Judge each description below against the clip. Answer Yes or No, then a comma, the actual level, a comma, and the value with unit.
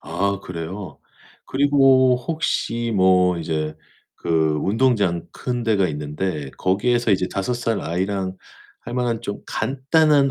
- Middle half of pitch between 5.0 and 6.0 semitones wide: Yes, wide, 5.4 semitones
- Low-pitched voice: Yes, low, 100 Hz